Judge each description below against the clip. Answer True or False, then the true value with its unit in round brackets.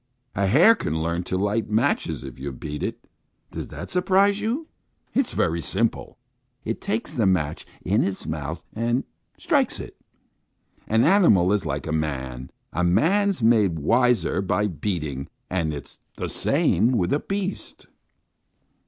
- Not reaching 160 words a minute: True (150 wpm)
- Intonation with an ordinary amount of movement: False (7.8 semitones)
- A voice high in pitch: False (95 Hz)